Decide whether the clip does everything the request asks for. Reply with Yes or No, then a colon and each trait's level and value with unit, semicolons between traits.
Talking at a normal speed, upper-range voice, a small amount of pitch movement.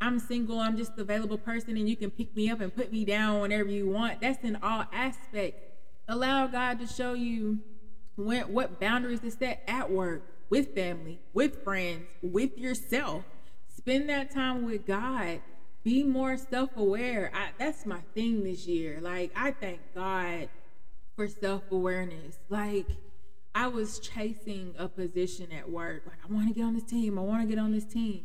No: average, 175 wpm; high, 215 Hz; average, 4.1 semitones